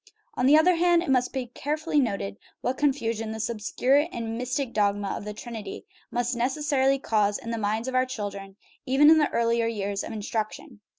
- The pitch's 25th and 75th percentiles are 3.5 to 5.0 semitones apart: Yes, average, 4.1 semitones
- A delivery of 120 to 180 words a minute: No, average, 190 wpm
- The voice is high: Yes, high, 235 Hz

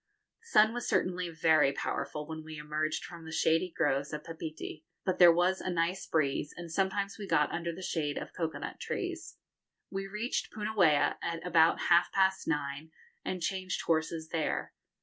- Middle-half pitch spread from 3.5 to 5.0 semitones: No, average, 3.0 semitones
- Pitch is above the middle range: No, medium, 165 Hz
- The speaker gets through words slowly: No, average, 175 wpm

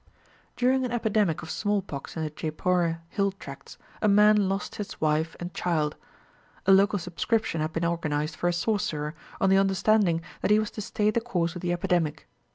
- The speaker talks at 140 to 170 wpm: No, average, 185 wpm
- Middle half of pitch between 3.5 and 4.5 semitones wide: Yes, average, 4.1 semitones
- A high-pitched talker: No, medium, 180 Hz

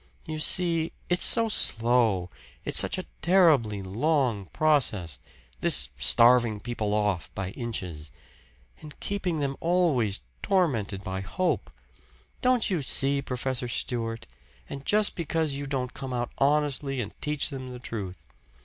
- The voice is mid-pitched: No, low, 130 Hz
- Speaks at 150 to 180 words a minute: No, slow, 135 wpm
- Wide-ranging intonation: Yes, wide, 6.6 semitones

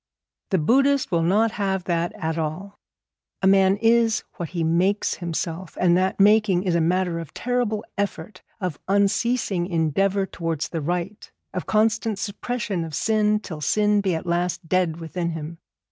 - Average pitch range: Yes, average, 3.7 semitones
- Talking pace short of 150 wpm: No, average, 160 wpm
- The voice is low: No, medium, 185 Hz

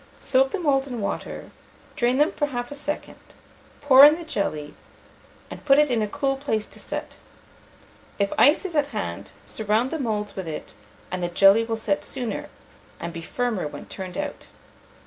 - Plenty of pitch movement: Yes, wide, 6.3 semitones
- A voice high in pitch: Yes, high, 245 Hz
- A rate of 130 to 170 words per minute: No, average, 185 wpm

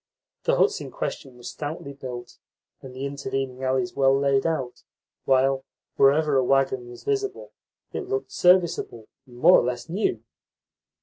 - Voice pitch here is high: No, low, 135 Hz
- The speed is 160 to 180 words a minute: No, average, 150 wpm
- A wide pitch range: No, average, 4.2 semitones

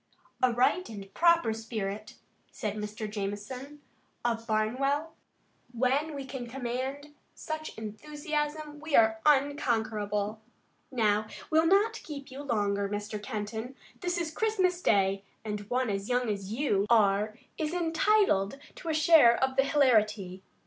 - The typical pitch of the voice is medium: No, high, 245 Hz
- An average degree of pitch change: No, wide, 5.9 semitones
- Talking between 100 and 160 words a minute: Yes, slow, 135 wpm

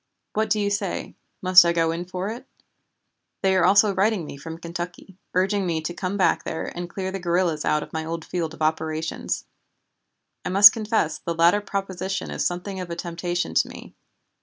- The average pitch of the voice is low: No, medium, 180 Hz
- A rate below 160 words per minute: No, average, 195 wpm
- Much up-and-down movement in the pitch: No, average, 2.8 semitones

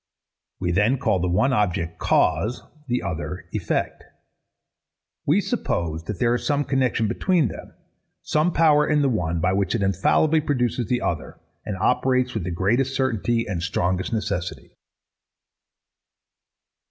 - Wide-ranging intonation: Yes, wide, 6.5 semitones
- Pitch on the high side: No, low, 110 Hz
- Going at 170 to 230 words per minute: No, average, 140 wpm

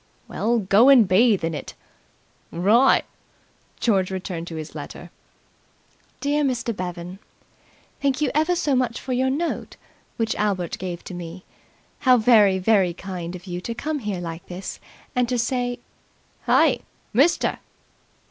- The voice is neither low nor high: No, high, 210 Hz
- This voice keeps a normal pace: Yes, average, 145 wpm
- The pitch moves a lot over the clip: Yes, wide, 5.7 semitones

